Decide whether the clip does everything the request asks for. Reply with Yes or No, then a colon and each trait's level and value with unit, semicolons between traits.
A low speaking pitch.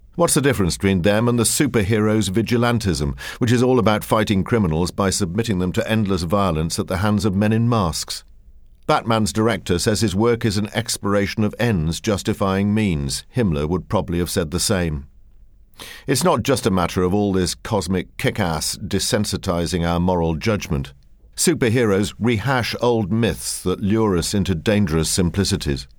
Yes: low, 100 Hz